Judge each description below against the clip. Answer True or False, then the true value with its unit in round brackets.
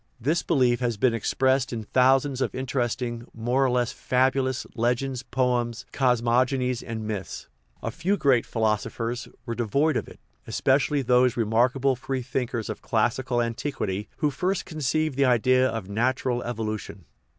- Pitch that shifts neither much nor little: False (2.2 semitones)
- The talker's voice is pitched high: False (125 Hz)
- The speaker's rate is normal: True (160 wpm)